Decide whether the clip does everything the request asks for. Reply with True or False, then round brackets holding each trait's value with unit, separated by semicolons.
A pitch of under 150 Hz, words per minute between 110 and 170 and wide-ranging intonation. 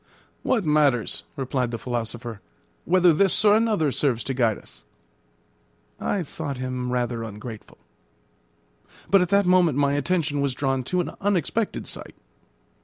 True (140 Hz; 140 wpm; 6.7 semitones)